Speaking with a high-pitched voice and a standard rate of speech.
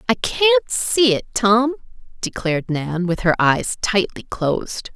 Yes: high, 220 Hz; average, 145 wpm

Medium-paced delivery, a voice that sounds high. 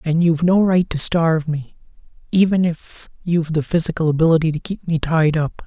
No: average, 190 wpm; medium, 165 Hz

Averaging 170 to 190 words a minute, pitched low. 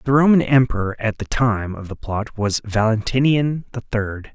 Yes: average, 180 wpm; low, 115 Hz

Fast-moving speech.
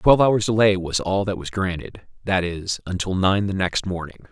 No: average, 195 wpm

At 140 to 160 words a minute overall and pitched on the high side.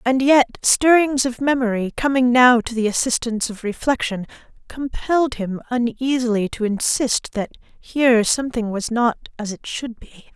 Yes: average, 150 wpm; high, 240 Hz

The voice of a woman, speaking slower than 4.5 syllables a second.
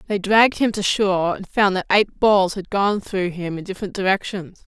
No: female; 5.2 syllables/s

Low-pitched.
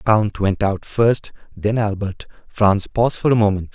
Yes: low, 105 Hz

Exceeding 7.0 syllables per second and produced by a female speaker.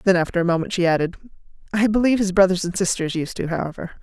Yes: 7.4 syllables/s; female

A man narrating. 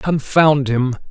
Yes: male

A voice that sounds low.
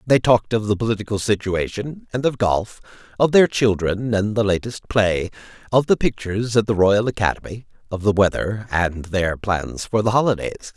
Yes: low, 105 Hz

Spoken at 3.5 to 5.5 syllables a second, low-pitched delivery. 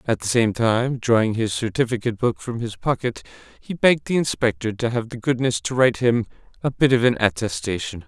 No: 5.7 syllables/s; low, 120 Hz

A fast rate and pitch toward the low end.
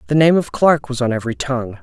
Yes: fast, 260 wpm; low, 130 Hz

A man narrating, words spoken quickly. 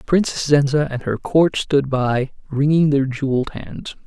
No: male; average, 160 wpm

